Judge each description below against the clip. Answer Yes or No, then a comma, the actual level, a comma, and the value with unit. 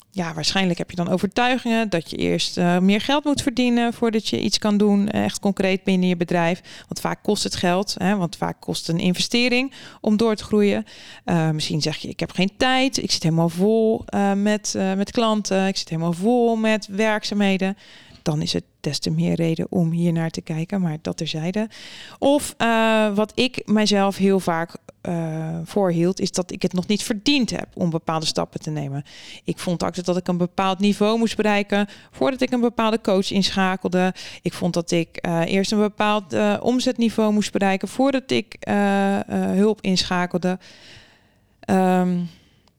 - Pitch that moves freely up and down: No, average, 3.7 semitones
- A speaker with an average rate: Yes, average, 190 wpm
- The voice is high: Yes, high, 195 Hz